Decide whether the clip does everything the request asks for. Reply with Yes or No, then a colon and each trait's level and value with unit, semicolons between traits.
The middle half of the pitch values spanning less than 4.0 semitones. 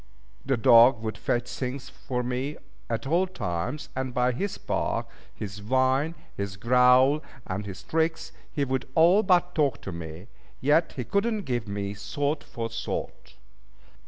No: average, 5.3 semitones